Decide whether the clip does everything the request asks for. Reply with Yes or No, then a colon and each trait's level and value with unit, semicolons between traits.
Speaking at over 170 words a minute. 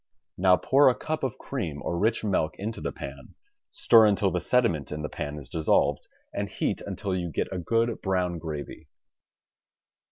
Yes: average, 180 wpm